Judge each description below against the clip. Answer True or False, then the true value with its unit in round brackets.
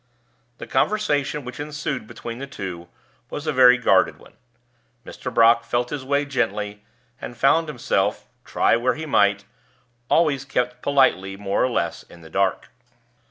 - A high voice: False (125 Hz)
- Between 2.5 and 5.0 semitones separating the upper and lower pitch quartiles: False (5.6 semitones)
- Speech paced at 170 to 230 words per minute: False (155 wpm)